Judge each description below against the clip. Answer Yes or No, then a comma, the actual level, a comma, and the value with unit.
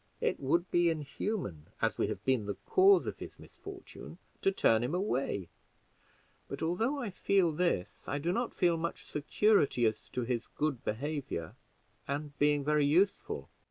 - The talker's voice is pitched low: No, medium, 150 Hz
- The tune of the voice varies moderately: No, wide, 6.3 semitones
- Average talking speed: Yes, average, 160 wpm